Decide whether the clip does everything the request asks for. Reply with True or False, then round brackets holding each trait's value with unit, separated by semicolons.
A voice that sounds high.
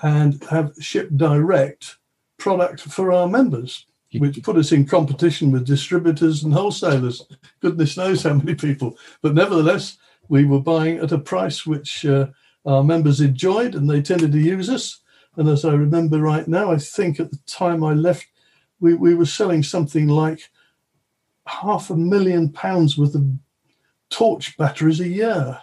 False (160 Hz)